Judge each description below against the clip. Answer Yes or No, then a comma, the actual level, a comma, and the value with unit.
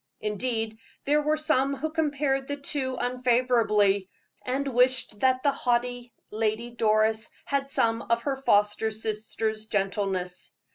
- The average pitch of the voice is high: Yes, high, 240 Hz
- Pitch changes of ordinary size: Yes, average, 3.8 semitones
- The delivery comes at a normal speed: No, slow, 130 wpm